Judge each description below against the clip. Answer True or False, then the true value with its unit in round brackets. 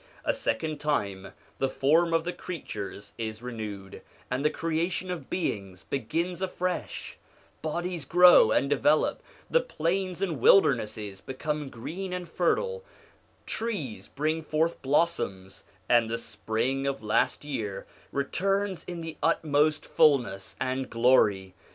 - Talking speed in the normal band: False (125 wpm)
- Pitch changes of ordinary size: False (7.1 semitones)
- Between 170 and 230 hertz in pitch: False (150 Hz)